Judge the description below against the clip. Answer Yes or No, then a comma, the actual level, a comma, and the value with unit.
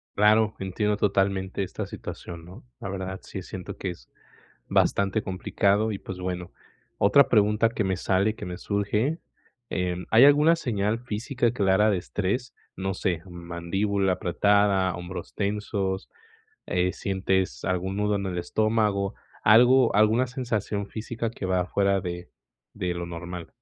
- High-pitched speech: No, low, 100 Hz